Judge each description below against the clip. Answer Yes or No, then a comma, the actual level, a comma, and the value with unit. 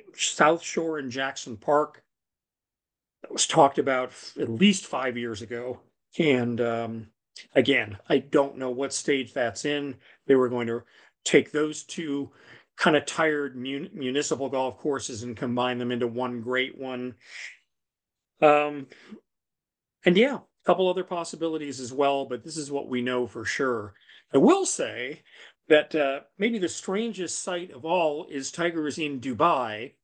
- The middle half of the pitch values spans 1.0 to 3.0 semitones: No, average, 4.0 semitones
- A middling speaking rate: Yes, average, 160 wpm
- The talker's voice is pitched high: No, medium, 140 Hz